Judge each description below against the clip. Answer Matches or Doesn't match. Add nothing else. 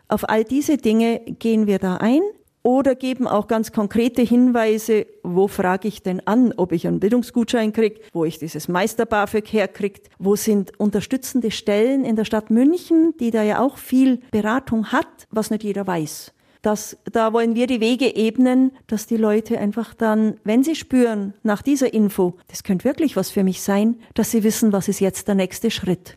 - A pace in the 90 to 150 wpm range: Doesn't match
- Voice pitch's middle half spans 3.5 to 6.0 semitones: Doesn't match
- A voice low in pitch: Doesn't match